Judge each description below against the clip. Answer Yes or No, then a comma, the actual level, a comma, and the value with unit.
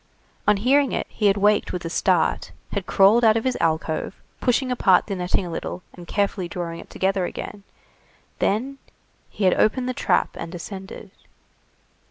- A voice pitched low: No, high, 200 Hz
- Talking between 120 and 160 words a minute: No, average, 175 wpm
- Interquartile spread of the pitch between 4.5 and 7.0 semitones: No, average, 4.0 semitones